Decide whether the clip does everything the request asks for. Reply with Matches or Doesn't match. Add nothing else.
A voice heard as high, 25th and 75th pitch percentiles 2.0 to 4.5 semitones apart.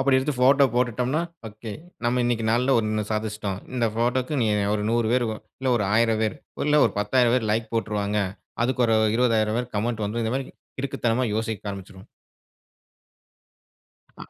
Doesn't match